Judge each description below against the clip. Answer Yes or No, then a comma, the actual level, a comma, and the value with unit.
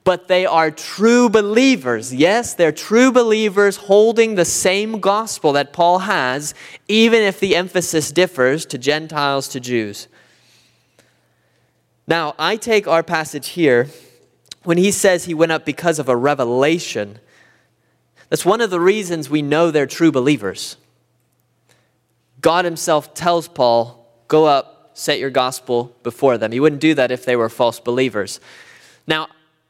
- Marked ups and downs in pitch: Yes, wide, 6.4 semitones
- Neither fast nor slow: Yes, average, 145 wpm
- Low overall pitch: No, medium, 155 Hz